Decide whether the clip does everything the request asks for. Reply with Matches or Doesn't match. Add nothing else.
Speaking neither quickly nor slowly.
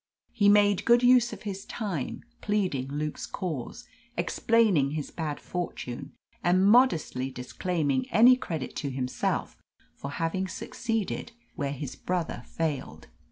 Doesn't match